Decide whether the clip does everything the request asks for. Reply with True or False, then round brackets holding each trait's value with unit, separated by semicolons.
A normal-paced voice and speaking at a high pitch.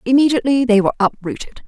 True (145 wpm; 235 Hz)